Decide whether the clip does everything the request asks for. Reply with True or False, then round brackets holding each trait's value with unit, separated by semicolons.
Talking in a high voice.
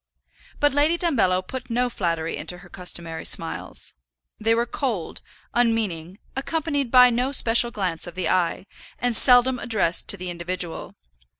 True (225 Hz)